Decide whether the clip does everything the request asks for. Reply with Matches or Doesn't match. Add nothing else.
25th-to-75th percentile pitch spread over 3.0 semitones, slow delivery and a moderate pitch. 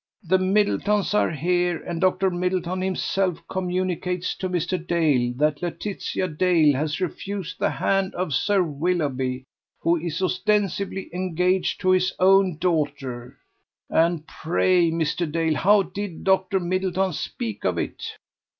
Doesn't match